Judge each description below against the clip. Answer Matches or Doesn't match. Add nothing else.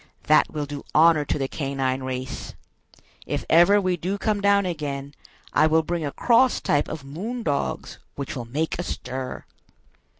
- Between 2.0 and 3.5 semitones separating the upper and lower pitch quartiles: Doesn't match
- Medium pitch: Matches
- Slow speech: Doesn't match